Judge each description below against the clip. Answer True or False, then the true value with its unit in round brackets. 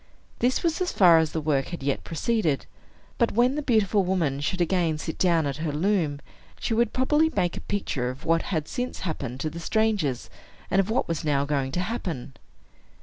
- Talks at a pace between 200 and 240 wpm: True (205 wpm)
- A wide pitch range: True (6.8 semitones)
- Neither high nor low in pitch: True (170 Hz)